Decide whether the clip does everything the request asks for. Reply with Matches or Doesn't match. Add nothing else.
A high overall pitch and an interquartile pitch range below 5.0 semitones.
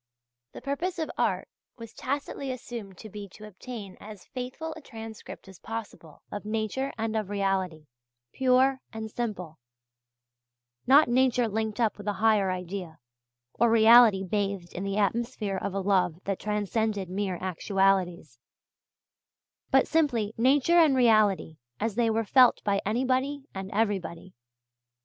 Matches